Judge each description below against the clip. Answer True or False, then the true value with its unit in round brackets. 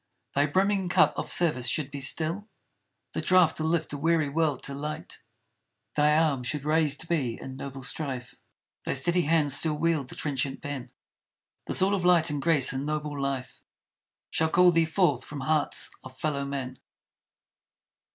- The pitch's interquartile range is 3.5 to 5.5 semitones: False (3.0 semitones)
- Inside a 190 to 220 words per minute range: False (165 wpm)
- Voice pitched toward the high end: False (150 Hz)